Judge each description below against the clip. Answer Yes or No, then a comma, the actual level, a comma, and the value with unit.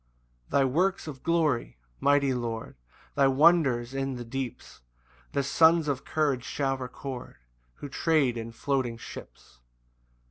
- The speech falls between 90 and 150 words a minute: Yes, slow, 135 wpm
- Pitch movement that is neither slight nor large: Yes, average, 3.1 semitones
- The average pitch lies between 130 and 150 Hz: Yes, low, 135 Hz